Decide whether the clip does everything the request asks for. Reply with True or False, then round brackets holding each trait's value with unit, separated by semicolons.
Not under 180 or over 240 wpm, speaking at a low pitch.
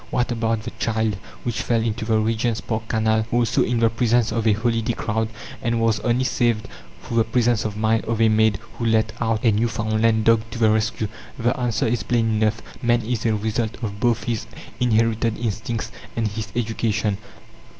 True (190 wpm; 115 Hz)